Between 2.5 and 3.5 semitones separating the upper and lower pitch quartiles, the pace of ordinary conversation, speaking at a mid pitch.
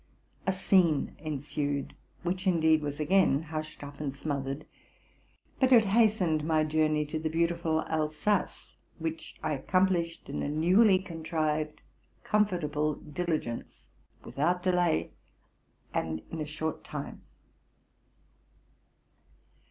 No: average, 2.9 semitones; slow, 115 wpm; medium, 160 Hz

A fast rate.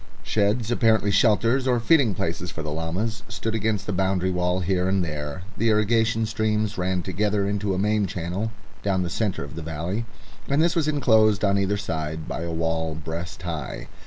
No: average, 190 wpm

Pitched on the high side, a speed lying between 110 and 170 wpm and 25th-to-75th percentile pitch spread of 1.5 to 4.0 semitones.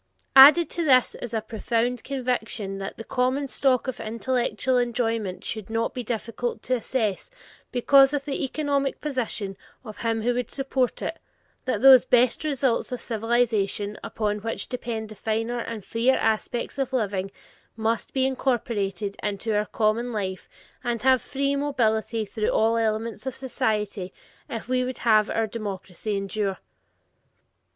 Yes: high, 230 Hz; average, 150 wpm; average, 3.0 semitones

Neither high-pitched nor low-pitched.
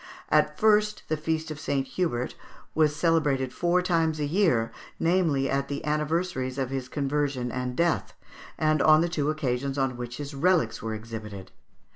Yes: medium, 145 Hz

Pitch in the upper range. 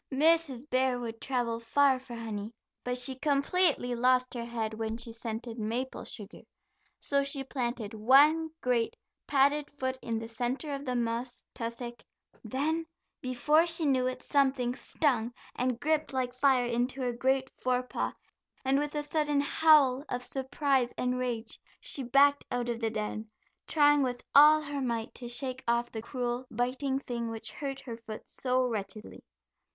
Yes: very high, 255 Hz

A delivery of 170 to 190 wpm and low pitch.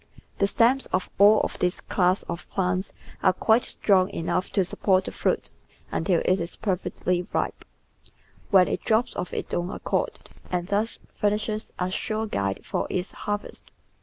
No: average, 175 wpm; high, 190 Hz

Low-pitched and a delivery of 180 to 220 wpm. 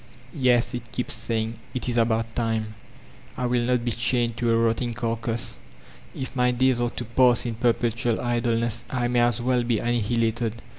Yes: low, 120 Hz; average, 190 wpm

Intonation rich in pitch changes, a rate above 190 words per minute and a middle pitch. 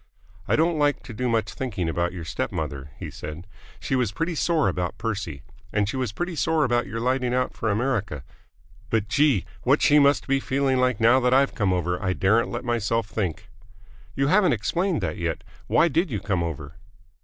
No: wide, 6.3 semitones; average, 200 wpm; low, 115 Hz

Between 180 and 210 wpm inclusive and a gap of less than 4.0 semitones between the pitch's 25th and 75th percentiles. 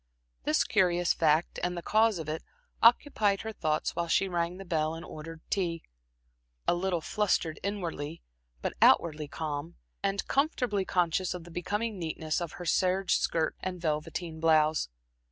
No: average, 155 wpm; average, 3.3 semitones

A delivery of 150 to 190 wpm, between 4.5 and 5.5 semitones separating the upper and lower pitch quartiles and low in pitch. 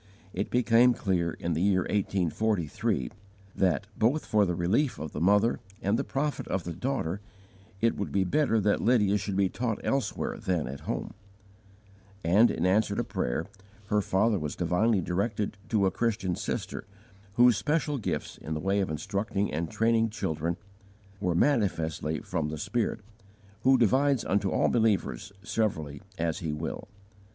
Yes: average, 160 wpm; average, 4.8 semitones; low, 100 Hz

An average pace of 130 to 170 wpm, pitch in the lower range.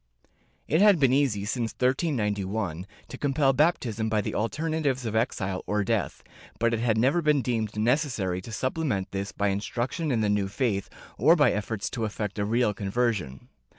No: average, 180 wpm; low, 115 Hz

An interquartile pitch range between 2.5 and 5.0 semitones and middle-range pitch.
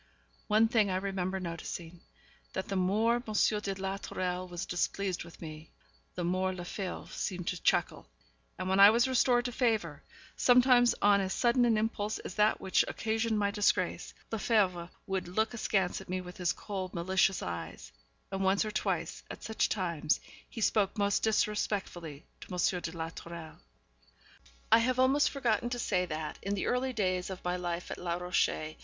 No: average, 3.6 semitones; high, 195 Hz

